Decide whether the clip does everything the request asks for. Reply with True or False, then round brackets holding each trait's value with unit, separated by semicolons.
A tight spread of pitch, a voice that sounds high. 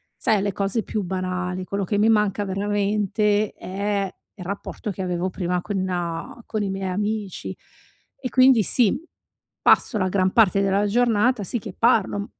True (2.2 semitones; 200 Hz)